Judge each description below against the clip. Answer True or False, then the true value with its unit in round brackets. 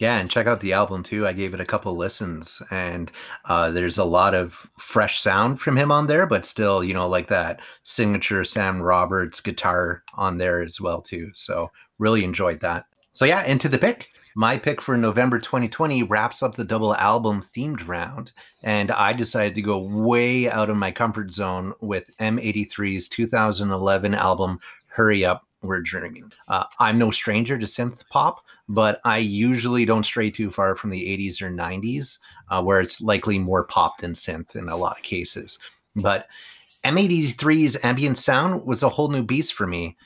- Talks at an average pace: True (185 wpm)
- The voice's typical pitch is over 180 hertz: False (105 Hz)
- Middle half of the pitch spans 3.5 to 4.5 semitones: True (4.1 semitones)